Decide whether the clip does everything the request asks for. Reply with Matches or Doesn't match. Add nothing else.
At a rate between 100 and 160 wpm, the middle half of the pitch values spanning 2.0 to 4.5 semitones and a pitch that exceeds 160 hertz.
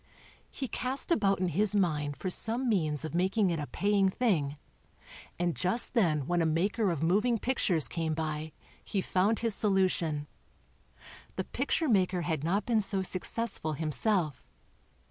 Doesn't match